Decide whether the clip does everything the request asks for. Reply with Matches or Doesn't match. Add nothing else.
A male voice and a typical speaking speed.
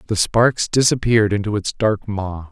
Matches